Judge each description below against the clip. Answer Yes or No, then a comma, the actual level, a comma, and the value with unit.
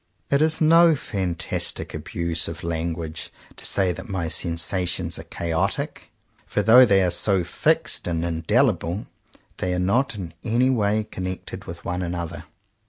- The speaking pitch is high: No, very low, 90 Hz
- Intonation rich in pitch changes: No, average, 4.2 semitones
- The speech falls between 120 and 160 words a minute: Yes, average, 155 wpm